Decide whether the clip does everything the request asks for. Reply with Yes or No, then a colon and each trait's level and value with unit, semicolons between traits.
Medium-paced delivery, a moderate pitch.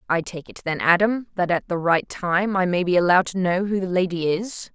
No: fast, 255 wpm; medium, 180 Hz